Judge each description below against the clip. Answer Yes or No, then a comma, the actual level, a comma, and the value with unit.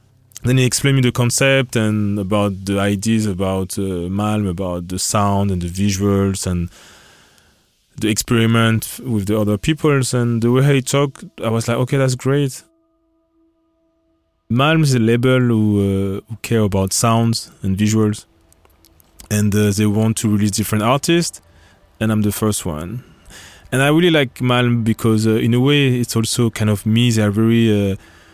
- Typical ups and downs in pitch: Yes, average, 3.9 semitones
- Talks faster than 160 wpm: Yes, average, 170 wpm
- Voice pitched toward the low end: Yes, low, 110 Hz